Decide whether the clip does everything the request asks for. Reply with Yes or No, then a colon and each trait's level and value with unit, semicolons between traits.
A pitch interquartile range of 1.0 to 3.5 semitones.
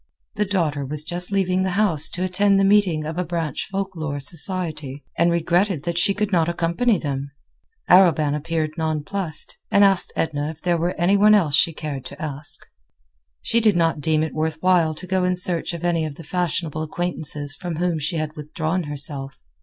Yes: average, 3.1 semitones